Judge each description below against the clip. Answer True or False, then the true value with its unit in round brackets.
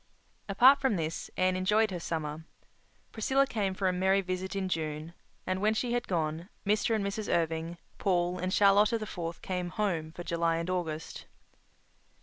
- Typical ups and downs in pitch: True (3.6 semitones)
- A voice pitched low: False (185 Hz)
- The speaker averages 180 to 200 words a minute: False (170 wpm)